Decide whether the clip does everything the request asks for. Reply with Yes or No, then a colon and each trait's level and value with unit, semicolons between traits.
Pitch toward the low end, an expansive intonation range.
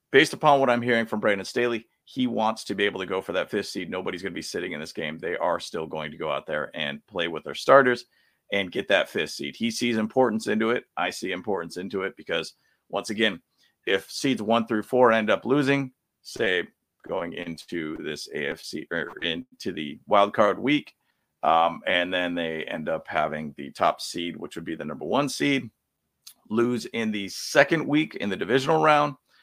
Yes: low, 120 Hz; wide, 5.9 semitones